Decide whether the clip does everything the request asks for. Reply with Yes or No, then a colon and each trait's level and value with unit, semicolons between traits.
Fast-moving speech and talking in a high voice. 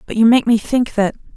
Yes: fast, 265 wpm; high, 225 Hz